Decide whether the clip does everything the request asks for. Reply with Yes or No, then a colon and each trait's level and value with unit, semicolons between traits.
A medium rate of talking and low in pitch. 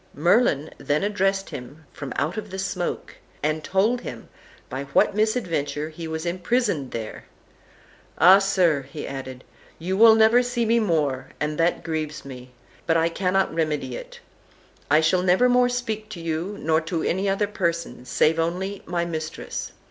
No: average, 160 wpm; medium, 170 Hz